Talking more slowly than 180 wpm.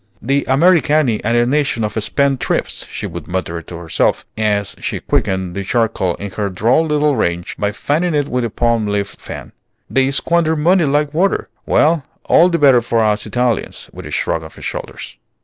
No: average, 190 wpm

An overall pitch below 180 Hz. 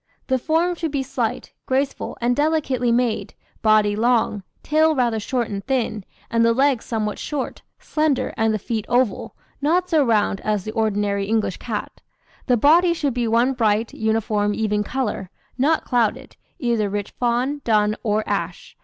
No: high, 235 Hz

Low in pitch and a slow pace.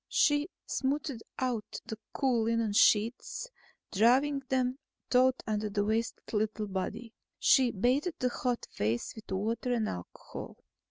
No: high, 230 Hz; slow, 130 wpm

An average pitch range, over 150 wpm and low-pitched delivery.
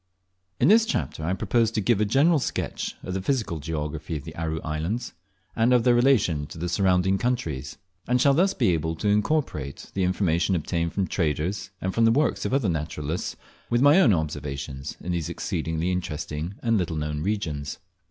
No: wide, 6.5 semitones; average, 190 wpm; very low, 90 Hz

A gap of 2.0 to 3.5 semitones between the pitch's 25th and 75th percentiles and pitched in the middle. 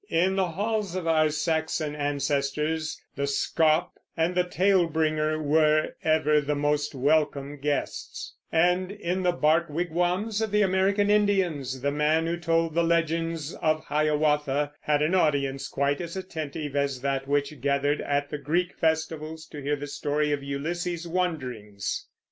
Yes: average, 2.9 semitones; medium, 155 Hz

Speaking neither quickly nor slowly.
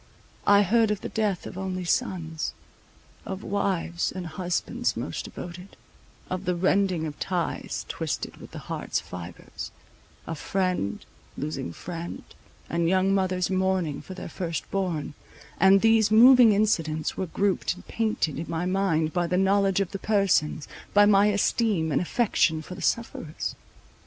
Yes: average, 150 wpm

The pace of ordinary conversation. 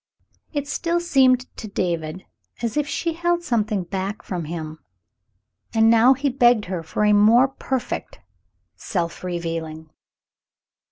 No: slow, 130 wpm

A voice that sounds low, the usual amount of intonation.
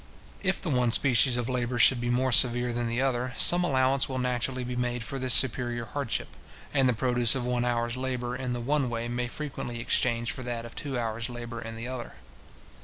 No: low, 125 Hz; narrow, 1.5 semitones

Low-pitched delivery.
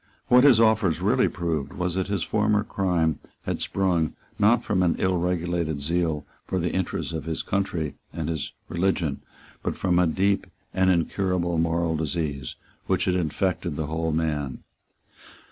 Yes: very low, 85 Hz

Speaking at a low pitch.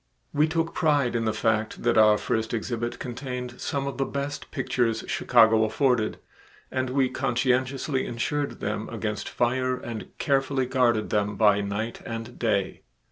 Yes: low, 125 Hz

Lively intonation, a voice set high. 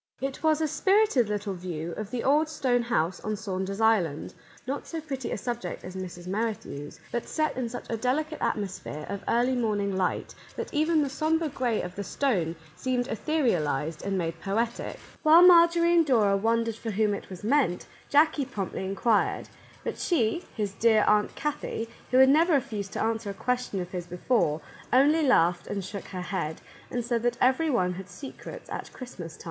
Yes: wide, 6.1 semitones; high, 225 Hz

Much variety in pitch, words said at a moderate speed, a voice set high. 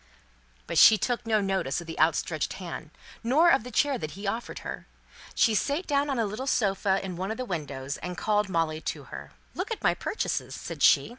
No: wide, 6.4 semitones; fast, 215 wpm; high, 200 Hz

